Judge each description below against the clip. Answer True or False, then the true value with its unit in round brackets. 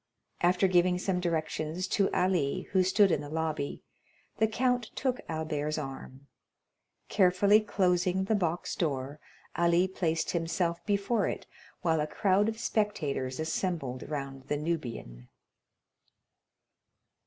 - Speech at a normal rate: False (120 wpm)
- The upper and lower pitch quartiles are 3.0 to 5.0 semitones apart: True (4.0 semitones)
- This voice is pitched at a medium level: True (170 Hz)